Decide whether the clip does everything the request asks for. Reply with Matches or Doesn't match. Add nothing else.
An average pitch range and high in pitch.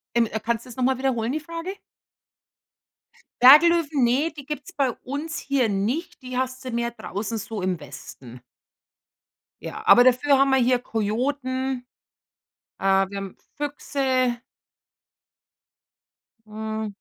Matches